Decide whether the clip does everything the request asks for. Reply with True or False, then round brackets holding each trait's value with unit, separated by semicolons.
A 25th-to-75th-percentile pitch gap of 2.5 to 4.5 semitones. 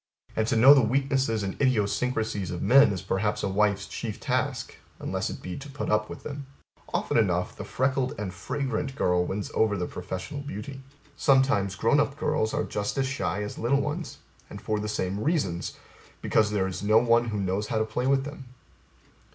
False (5.1 semitones)